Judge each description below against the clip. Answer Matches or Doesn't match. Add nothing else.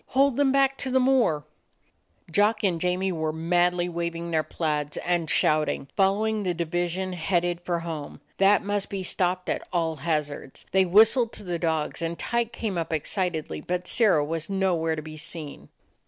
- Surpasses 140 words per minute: Matches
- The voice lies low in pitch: Doesn't match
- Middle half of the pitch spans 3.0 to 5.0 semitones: Matches